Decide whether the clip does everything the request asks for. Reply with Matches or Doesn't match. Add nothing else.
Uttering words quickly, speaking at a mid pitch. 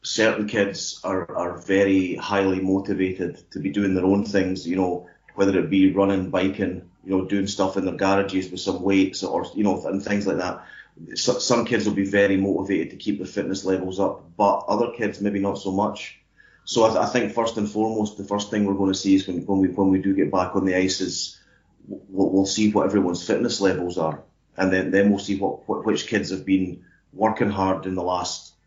Doesn't match